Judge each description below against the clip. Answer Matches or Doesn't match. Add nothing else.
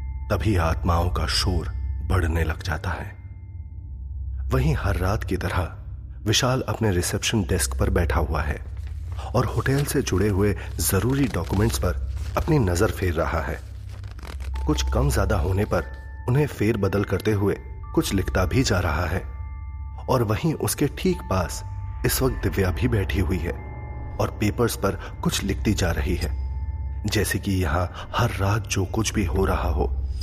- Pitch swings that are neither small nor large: Matches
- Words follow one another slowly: Doesn't match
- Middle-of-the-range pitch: Doesn't match